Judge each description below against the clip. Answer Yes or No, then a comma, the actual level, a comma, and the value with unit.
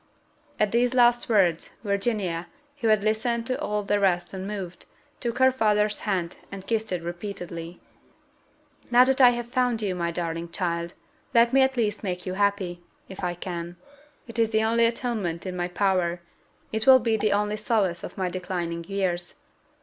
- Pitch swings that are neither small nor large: Yes, average, 4.5 semitones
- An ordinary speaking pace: Yes, average, 175 wpm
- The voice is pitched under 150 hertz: No, high, 200 Hz